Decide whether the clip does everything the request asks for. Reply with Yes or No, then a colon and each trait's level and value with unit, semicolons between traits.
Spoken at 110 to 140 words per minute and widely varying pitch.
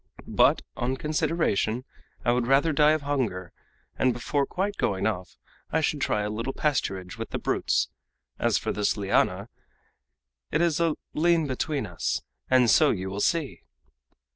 No: average, 160 wpm; wide, 6.6 semitones